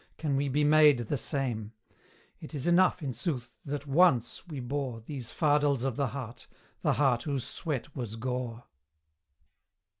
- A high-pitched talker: No, low, 135 Hz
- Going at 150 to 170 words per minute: Yes, average, 155 wpm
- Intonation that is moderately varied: Yes, average, 3.4 semitones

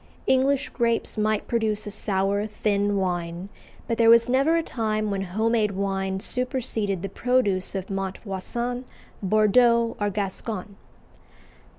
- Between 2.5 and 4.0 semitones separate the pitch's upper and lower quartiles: Yes, average, 3.2 semitones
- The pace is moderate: No, slow, 130 wpm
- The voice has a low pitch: No, high, 210 Hz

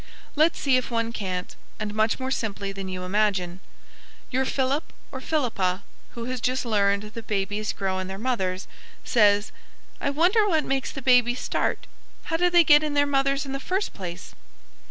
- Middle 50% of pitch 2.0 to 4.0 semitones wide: No, wide, 5.5 semitones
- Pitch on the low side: No, high, 235 Hz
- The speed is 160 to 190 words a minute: Yes, average, 180 wpm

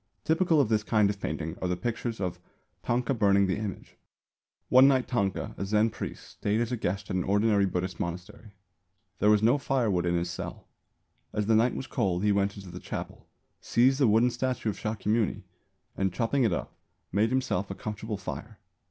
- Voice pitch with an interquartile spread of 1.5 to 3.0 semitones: No, average, 3.5 semitones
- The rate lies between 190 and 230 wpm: Yes, average, 195 wpm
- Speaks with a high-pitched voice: No, low, 105 Hz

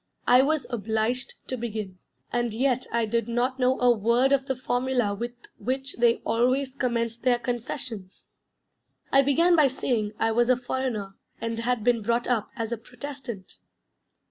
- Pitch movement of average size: No, narrow, 2.2 semitones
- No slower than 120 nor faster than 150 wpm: No, average, 165 wpm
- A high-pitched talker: Yes, high, 240 Hz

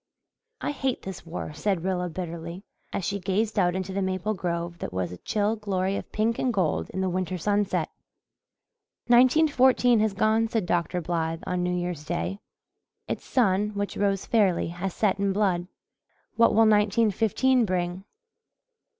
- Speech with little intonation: No, average, 3.4 semitones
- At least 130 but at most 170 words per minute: Yes, average, 165 wpm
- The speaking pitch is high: Yes, high, 195 Hz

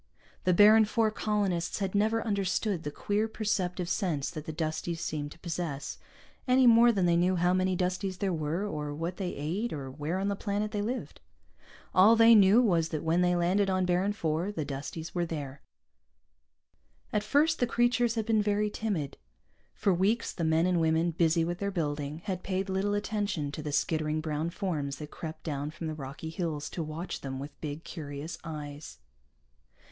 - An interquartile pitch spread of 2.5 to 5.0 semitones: Yes, average, 4.7 semitones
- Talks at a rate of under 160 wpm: No, average, 190 wpm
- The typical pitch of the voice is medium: Yes, medium, 175 Hz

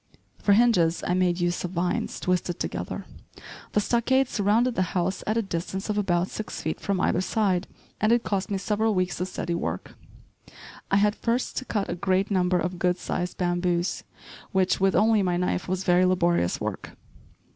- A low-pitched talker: No, medium, 185 Hz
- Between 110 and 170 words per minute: No, average, 185 wpm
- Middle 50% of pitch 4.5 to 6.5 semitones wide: No, average, 2.7 semitones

